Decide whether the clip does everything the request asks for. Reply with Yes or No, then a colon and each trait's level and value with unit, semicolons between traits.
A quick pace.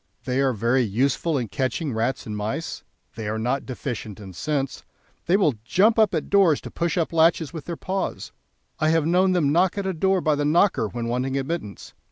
Yes: fast, 210 wpm